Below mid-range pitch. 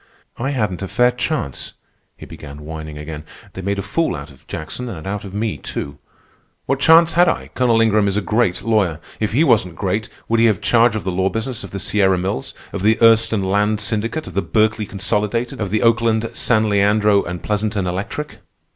Yes: low, 105 Hz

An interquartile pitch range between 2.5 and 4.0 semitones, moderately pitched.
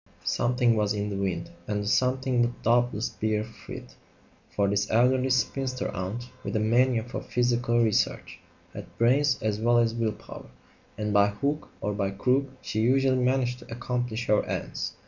No: average, 3.0 semitones; low, 120 Hz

